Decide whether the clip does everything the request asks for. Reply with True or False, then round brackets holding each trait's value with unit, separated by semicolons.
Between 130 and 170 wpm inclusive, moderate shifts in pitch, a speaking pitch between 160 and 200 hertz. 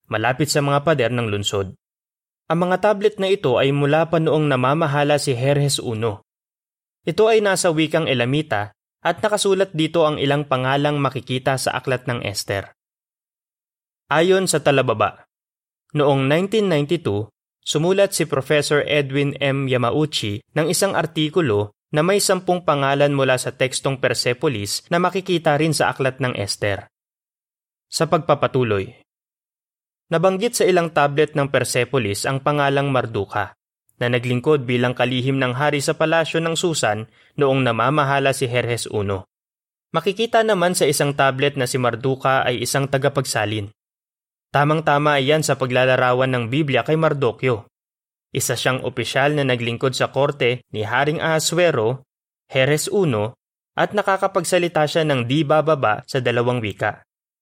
False (135 wpm; 4.2 semitones; 140 Hz)